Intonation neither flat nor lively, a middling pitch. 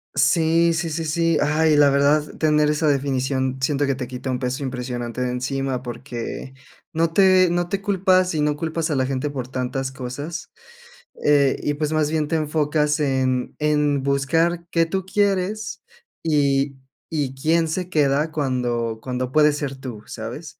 Yes: average, 3.5 semitones; medium, 145 Hz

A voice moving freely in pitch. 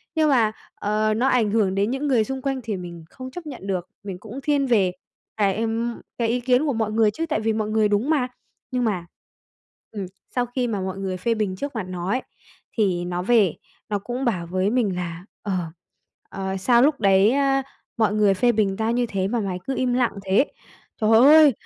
No: average, 4.3 semitones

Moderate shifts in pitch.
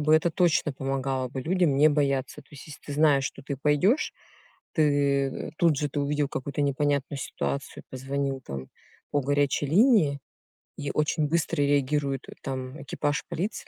No: narrow, 1.7 semitones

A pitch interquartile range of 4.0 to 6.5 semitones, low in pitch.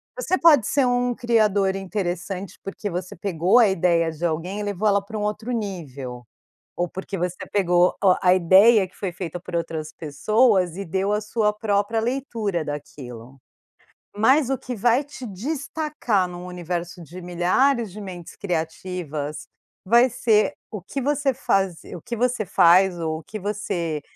No: average, 4.3 semitones; high, 195 Hz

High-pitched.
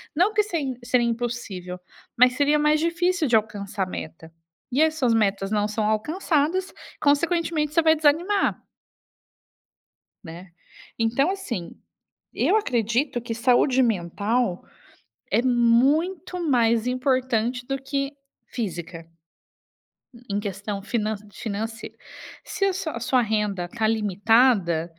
Yes: high, 240 Hz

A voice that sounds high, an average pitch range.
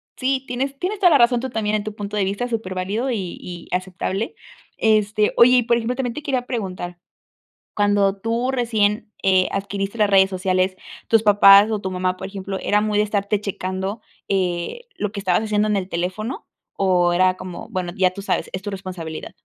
Yes: high, 205 Hz; average, 3.2 semitones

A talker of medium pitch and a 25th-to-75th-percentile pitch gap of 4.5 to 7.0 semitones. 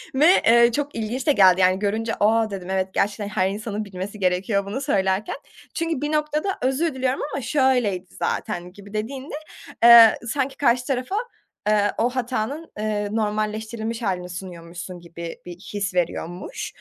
No: high, 215 Hz; average, 5.0 semitones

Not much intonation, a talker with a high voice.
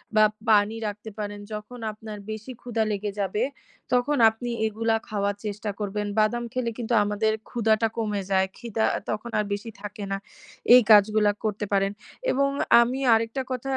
Yes: narrow, 2.1 semitones; high, 215 Hz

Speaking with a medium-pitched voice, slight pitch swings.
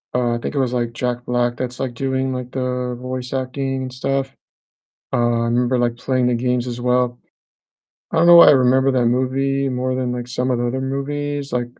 No: low, 125 Hz; narrow, 1.3 semitones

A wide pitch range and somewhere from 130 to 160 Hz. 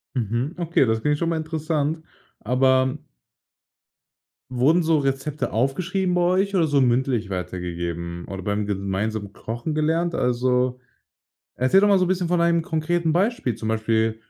Yes: wide, 6.9 semitones; low, 135 Hz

